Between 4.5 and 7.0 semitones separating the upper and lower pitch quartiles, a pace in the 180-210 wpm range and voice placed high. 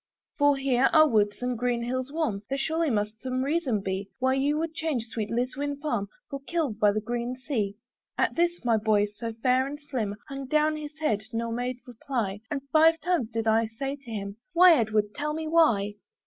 Yes: average, 5.2 semitones; fast, 205 wpm; very high, 255 Hz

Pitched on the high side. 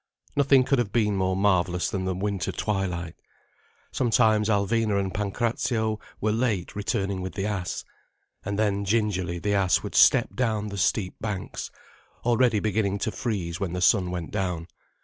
No: low, 100 Hz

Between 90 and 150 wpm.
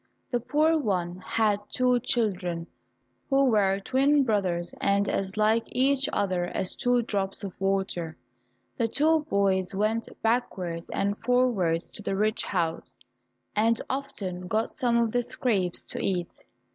Yes: average, 145 wpm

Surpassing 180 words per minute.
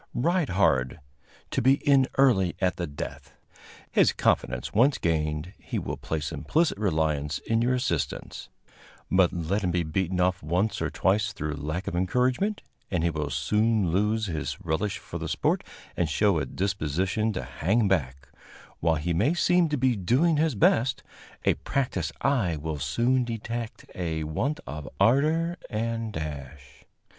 No: average, 160 wpm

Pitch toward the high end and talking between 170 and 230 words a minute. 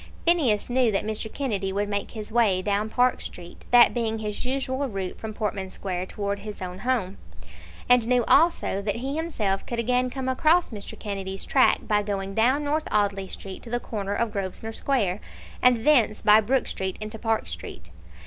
Yes: high, 215 Hz; average, 185 wpm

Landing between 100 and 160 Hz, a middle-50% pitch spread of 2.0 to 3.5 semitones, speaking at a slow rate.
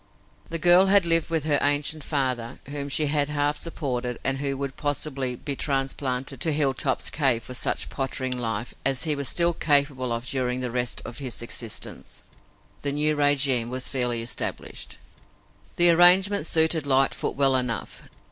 No: medium, 140 Hz; average, 3.0 semitones; average, 165 wpm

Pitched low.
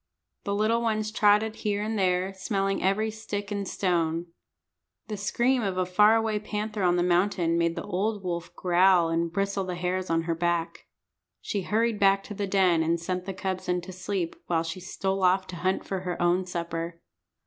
No: high, 190 Hz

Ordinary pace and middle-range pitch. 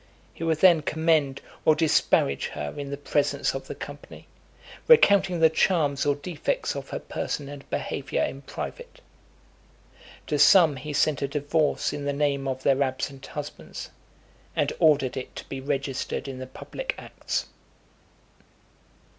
Yes: average, 150 wpm; medium, 145 Hz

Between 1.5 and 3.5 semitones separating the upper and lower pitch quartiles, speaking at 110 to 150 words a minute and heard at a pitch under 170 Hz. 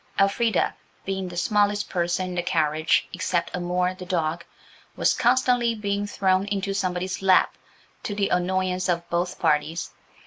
No: narrow, 2.4 semitones; average, 140 wpm; medium, 185 Hz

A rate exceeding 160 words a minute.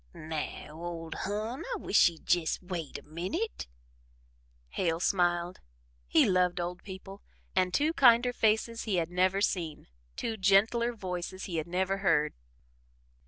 No: average, 140 wpm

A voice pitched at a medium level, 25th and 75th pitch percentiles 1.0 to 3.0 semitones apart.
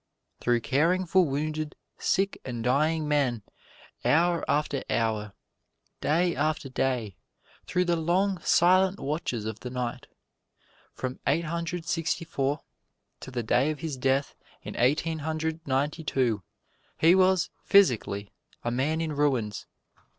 No: medium, 150 Hz; average, 4.7 semitones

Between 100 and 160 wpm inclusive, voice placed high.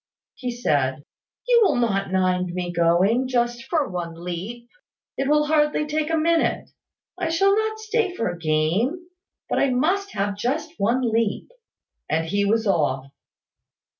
Yes: average, 155 wpm; high, 235 Hz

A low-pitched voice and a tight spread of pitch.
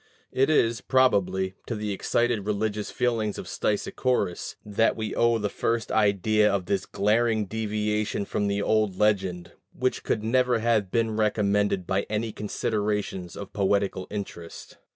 Yes: low, 105 Hz; narrow, 1.9 semitones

